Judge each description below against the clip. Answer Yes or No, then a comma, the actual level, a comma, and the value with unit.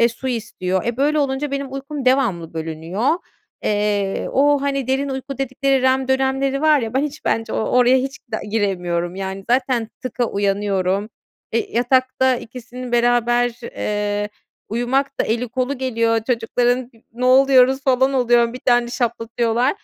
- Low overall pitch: No, high, 245 Hz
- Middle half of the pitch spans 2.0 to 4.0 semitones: Yes, average, 3.0 semitones